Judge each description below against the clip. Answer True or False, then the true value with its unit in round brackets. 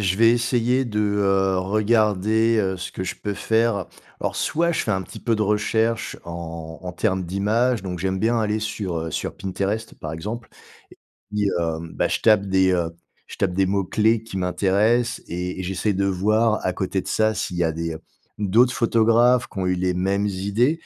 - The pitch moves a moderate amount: True (3.3 semitones)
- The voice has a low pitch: True (100 Hz)